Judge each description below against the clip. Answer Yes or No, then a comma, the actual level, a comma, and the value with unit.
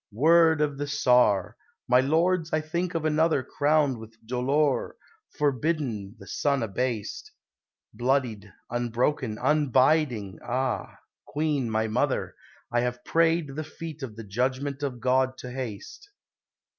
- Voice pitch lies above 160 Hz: No, low, 130 Hz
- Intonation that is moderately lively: Yes, average, 4.0 semitones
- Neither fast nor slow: No, slow, 130 wpm